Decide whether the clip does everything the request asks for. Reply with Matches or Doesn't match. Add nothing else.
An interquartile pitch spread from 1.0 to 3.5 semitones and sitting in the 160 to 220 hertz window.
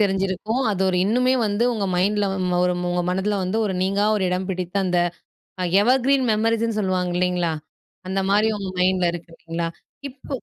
Matches